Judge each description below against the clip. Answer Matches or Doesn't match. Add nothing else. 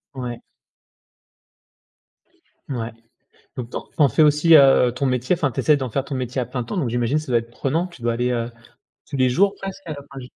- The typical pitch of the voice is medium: Doesn't match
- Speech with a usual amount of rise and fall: Matches